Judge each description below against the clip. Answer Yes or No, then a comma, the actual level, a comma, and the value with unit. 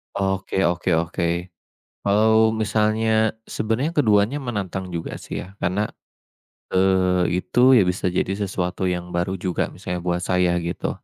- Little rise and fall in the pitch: No, average, 3.3 semitones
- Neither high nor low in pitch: No, very low, 95 Hz